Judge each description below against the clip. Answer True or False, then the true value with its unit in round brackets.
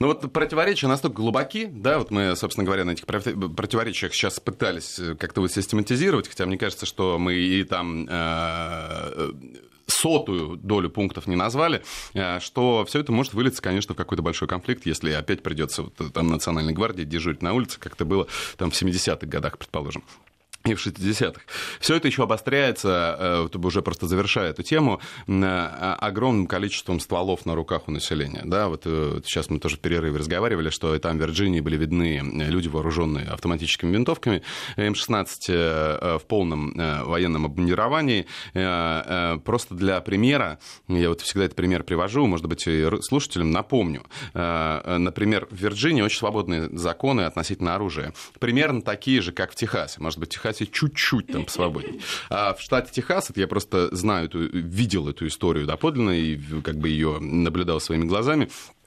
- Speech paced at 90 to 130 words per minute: False (155 wpm)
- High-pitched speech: False (90 Hz)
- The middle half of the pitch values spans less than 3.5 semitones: False (4.3 semitones)